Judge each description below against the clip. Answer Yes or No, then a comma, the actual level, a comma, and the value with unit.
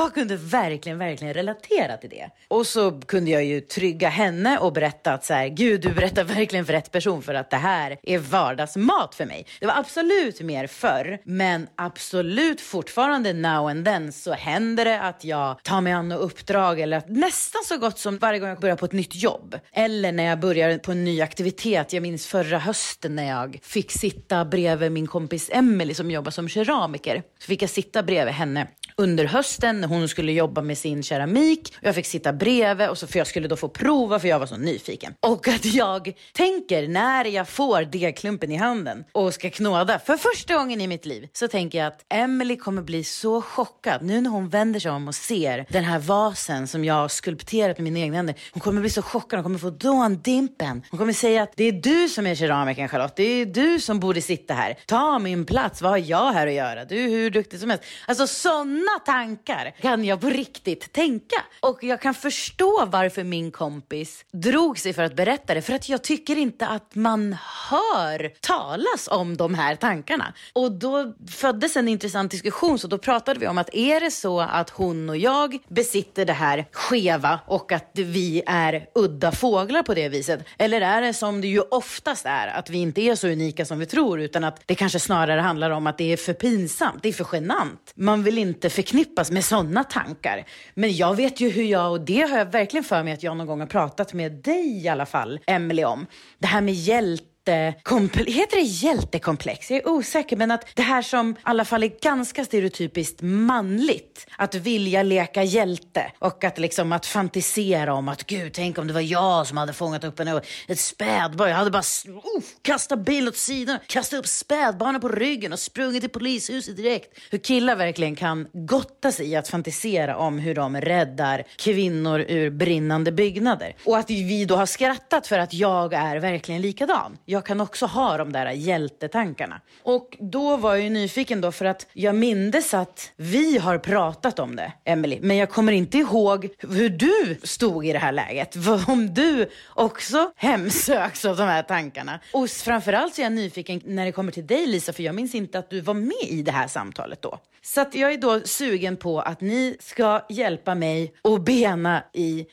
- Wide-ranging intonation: Yes, wide, 5.9 semitones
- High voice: Yes, high, 195 Hz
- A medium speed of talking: No, fast, 210 wpm